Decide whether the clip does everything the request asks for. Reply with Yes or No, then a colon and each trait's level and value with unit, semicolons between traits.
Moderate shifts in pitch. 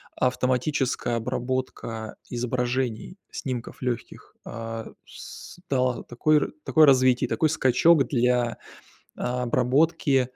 No: narrow, 1.7 semitones